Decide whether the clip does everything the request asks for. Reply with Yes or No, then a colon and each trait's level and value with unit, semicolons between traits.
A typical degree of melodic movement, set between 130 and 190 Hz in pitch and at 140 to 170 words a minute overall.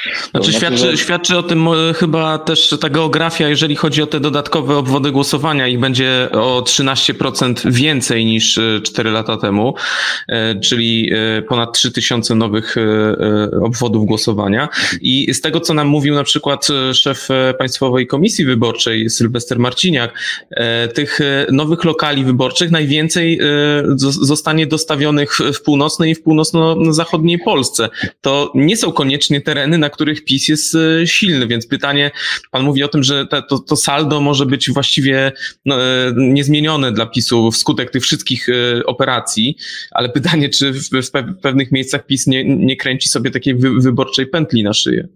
Yes: average, 3.4 semitones; medium, 140 Hz; average, 145 wpm